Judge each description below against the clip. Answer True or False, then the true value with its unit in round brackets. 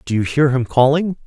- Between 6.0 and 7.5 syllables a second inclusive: False (5.4 syllables/s)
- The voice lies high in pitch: False (135 Hz)